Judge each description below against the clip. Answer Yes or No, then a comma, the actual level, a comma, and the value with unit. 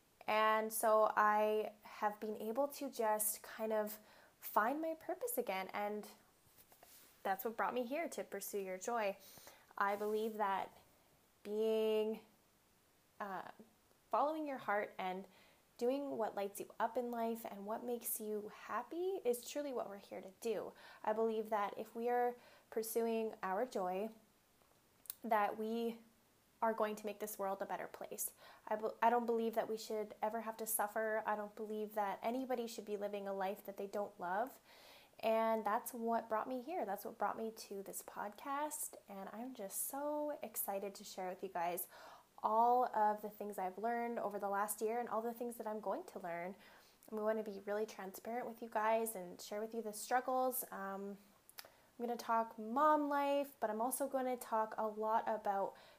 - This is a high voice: Yes, high, 220 Hz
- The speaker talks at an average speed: Yes, average, 185 wpm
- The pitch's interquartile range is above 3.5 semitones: No, narrow, 2.4 semitones